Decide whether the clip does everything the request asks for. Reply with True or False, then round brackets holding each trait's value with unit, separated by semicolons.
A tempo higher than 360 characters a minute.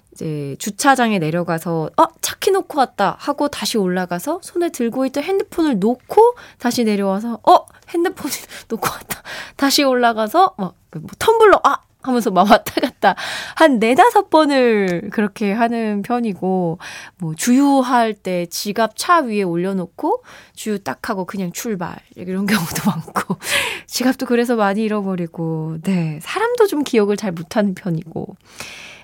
False (295 characters per minute)